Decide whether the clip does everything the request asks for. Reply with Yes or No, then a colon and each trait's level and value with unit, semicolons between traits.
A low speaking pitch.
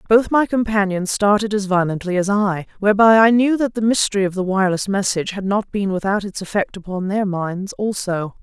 No: high, 200 Hz